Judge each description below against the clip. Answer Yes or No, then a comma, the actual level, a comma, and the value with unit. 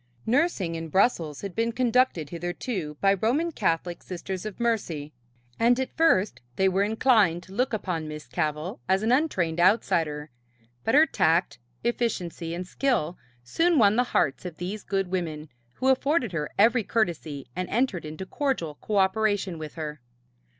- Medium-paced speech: Yes, average, 155 wpm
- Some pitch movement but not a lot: No, wide, 6.0 semitones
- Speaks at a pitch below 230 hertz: Yes, high, 190 Hz